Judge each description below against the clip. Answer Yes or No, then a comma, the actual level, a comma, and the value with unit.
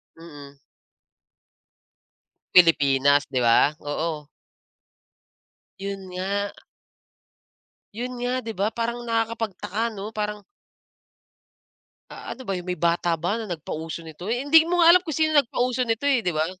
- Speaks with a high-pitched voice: Yes, high, 200 Hz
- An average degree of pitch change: No, wide, 6.3 semitones